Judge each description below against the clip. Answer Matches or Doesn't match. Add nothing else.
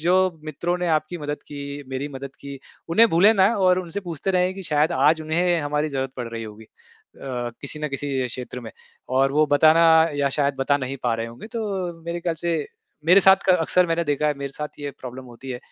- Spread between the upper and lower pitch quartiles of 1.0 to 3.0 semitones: Doesn't match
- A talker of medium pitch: Matches